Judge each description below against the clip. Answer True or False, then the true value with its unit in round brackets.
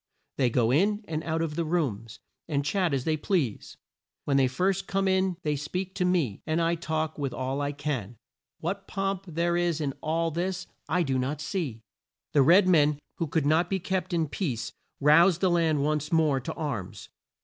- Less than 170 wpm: False (195 wpm)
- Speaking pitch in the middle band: True (160 Hz)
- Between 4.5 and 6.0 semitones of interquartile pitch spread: False (3.9 semitones)